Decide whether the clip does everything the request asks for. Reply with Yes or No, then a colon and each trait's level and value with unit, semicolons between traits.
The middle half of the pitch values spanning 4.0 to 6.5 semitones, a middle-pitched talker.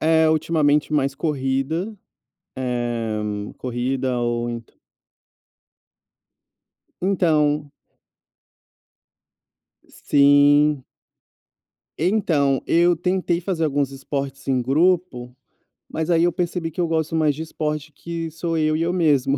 No: average, 3.5 semitones; medium, 150 Hz